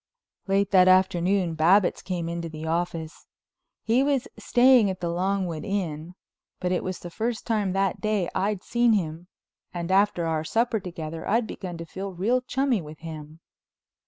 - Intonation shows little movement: No, average, 3.8 semitones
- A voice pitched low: No, medium, 185 Hz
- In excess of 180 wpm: No, average, 165 wpm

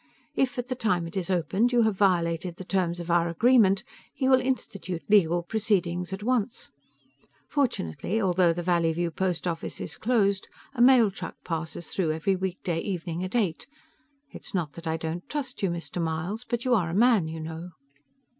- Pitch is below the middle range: No, medium, 185 Hz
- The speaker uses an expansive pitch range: No, average, 4.6 semitones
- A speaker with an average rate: Yes, average, 185 wpm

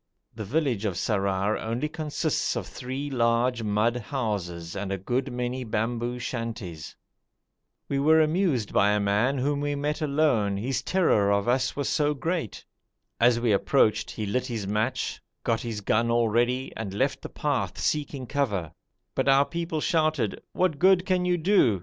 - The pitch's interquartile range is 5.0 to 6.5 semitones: Yes, average, 5.3 semitones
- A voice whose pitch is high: No, low, 120 Hz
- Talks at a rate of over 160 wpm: Yes, average, 170 wpm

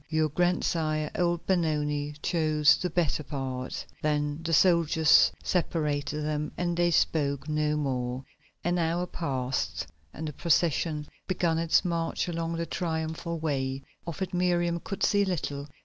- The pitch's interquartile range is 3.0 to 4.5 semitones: No, narrow, 2.6 semitones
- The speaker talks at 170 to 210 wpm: No, average, 140 wpm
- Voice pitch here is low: No, medium, 160 Hz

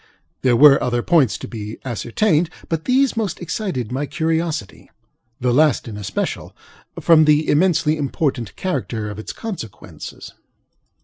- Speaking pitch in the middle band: Yes, medium, 150 Hz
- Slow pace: Yes, slow, 130 wpm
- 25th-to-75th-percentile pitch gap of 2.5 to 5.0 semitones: No, wide, 5.6 semitones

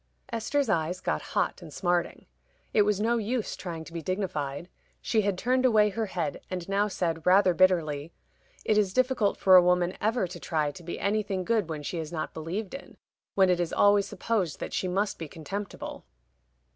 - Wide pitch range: No, average, 3.7 semitones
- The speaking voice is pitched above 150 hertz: Yes, medium, 185 Hz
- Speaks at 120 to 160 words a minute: No, average, 195 wpm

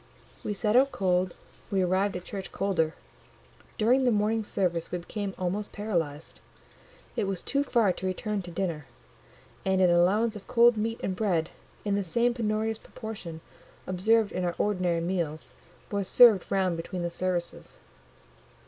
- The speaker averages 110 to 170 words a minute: Yes, average, 155 wpm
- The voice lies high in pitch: Yes, high, 195 Hz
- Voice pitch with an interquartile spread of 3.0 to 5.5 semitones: Yes, average, 3.3 semitones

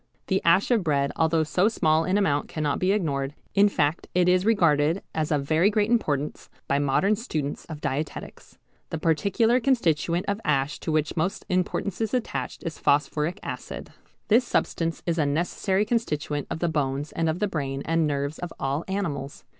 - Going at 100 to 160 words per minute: No, average, 185 wpm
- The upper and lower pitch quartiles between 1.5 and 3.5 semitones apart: No, average, 4.8 semitones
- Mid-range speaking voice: Yes, medium, 165 Hz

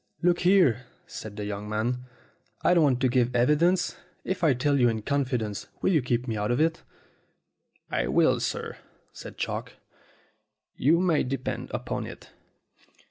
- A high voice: No, low, 125 Hz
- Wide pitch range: Yes, wide, 5.7 semitones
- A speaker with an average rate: Yes, average, 160 wpm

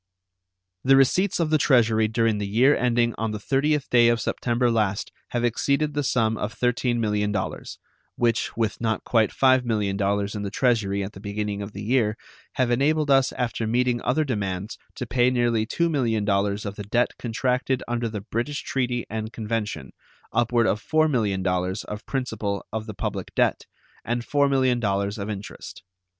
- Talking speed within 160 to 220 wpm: Yes, average, 170 wpm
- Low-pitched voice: Yes, low, 115 Hz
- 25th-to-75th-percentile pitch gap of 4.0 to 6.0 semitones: No, average, 3.3 semitones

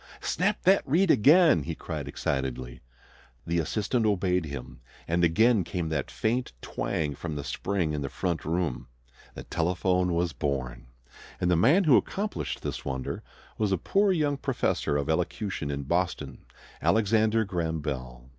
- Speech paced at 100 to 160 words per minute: Yes, average, 155 wpm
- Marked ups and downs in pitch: Yes, wide, 7.4 semitones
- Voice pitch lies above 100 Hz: No, very low, 85 Hz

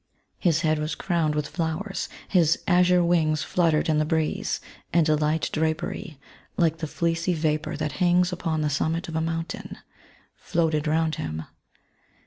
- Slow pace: No, average, 155 wpm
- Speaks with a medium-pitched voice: Yes, medium, 160 Hz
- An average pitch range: No, narrow, 1.8 semitones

